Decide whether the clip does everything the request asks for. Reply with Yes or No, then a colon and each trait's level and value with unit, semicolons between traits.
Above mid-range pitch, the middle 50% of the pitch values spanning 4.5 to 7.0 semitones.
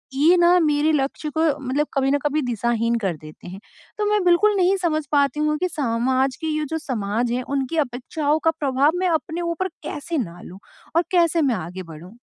Yes: very high, 290 Hz; average, 5.2 semitones